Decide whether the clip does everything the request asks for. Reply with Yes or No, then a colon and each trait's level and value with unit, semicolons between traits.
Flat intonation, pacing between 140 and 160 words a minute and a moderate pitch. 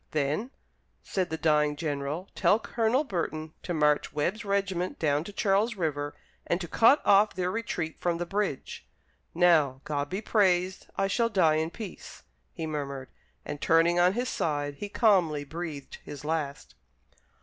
No: average, 4.7 semitones; average, 155 wpm; medium, 170 Hz